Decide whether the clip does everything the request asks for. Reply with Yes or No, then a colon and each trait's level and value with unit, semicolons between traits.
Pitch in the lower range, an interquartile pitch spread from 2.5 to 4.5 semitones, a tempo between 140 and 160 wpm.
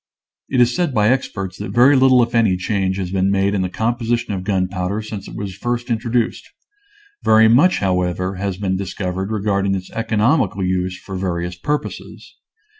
No: low, 100 Hz; average, 4.0 semitones; average, 175 wpm